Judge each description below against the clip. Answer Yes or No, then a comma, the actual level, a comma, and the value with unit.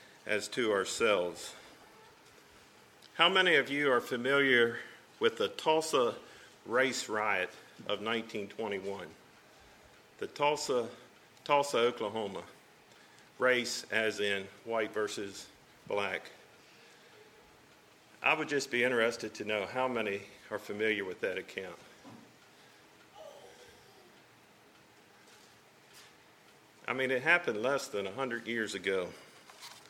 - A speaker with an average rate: No, slow, 100 wpm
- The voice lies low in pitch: Yes, low, 120 Hz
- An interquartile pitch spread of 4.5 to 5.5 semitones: Yes, average, 5.0 semitones